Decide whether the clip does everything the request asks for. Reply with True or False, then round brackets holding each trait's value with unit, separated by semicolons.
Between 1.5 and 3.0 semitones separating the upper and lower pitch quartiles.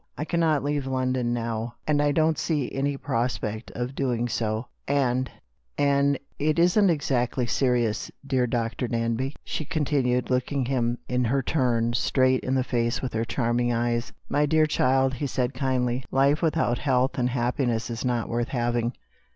True (2.7 semitones)